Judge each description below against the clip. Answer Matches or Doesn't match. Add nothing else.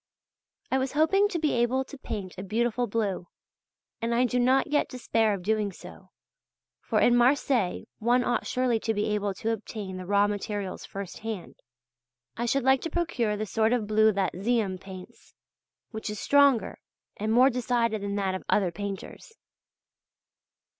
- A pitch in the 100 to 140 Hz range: Doesn't match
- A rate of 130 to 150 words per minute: Doesn't match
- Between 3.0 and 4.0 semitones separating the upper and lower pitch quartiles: Matches